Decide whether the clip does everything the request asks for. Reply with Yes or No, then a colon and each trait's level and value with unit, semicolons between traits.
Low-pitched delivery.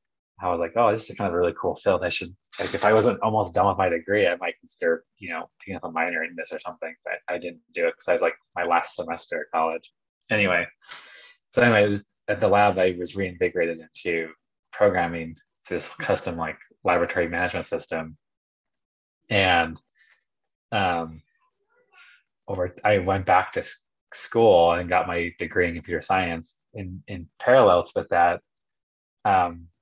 Yes: very low, 90 Hz